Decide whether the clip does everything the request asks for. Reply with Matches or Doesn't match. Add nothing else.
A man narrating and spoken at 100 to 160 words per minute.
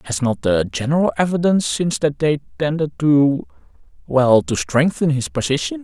Matches